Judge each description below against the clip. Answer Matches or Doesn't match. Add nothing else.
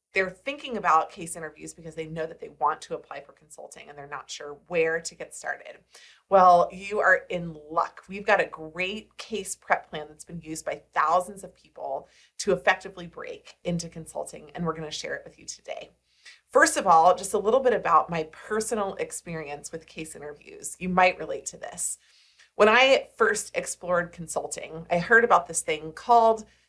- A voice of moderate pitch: Matches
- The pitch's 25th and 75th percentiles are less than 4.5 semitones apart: Matches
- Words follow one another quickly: Doesn't match